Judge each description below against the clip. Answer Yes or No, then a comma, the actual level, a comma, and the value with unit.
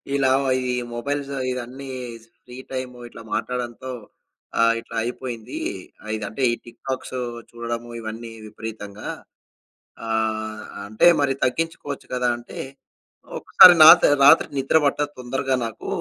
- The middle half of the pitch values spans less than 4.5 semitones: Yes, average, 2.8 semitones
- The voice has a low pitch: Yes, low, 125 Hz